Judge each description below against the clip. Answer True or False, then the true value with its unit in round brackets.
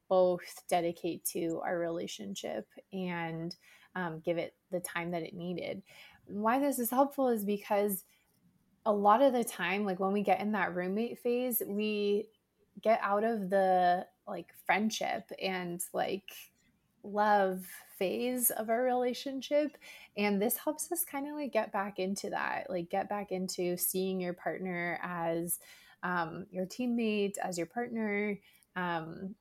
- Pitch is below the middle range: False (195 Hz)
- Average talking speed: True (150 wpm)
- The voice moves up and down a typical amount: True (3.8 semitones)